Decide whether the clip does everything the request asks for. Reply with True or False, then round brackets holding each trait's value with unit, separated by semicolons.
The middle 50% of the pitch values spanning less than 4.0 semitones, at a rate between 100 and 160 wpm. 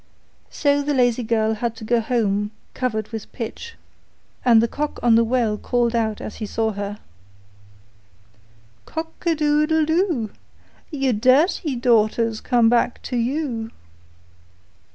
False (4.3 semitones; 135 wpm)